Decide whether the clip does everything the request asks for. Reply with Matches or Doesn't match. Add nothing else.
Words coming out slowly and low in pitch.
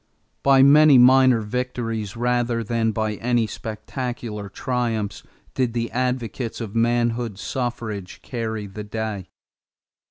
Matches